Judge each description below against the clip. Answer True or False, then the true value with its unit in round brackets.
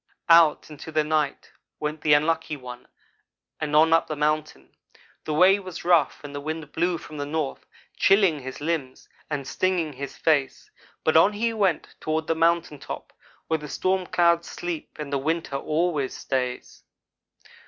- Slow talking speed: False (165 wpm)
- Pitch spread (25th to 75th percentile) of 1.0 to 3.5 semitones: True (2.5 semitones)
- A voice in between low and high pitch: True (155 Hz)